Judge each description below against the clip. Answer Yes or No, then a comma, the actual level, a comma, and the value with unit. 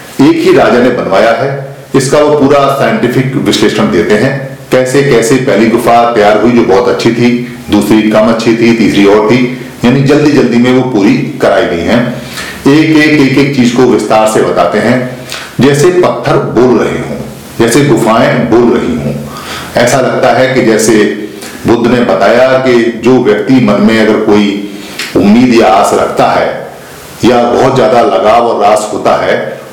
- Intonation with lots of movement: No, average, 3.1 semitones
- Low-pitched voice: Yes, low, 125 Hz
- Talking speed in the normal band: Yes, average, 175 wpm